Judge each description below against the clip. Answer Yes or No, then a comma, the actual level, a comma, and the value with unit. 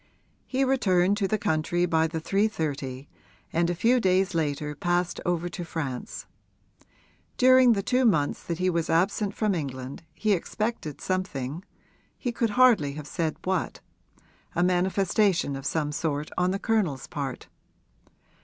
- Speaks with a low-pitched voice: No, medium, 175 Hz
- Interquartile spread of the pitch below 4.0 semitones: No, average, 4.8 semitones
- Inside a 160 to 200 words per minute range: No, average, 145 wpm